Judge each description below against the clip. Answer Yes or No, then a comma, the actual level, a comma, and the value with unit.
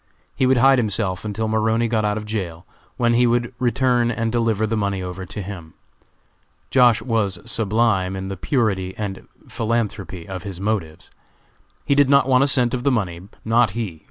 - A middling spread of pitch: Yes, average, 3.7 semitones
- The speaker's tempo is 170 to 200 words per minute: Yes, average, 185 wpm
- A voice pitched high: No, low, 110 Hz